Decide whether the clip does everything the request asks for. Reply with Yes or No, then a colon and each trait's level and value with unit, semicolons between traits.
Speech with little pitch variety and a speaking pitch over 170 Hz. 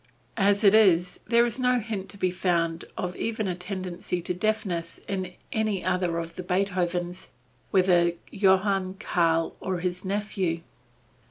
Yes: narrow, 2.3 semitones; medium, 185 Hz